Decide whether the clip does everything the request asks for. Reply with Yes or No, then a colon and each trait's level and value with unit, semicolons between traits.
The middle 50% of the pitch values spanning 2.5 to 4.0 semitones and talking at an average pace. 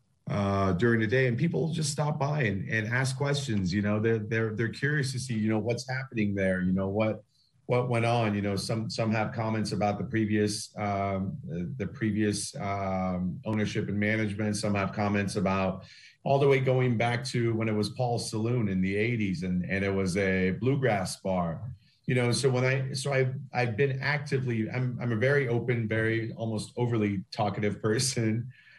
Yes: average, 3.5 semitones; average, 195 wpm